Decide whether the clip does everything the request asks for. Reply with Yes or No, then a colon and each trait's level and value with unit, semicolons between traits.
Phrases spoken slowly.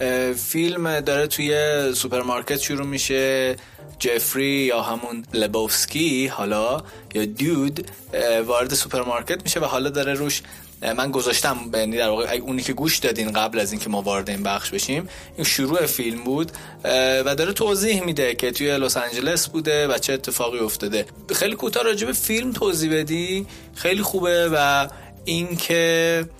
No: average, 150 wpm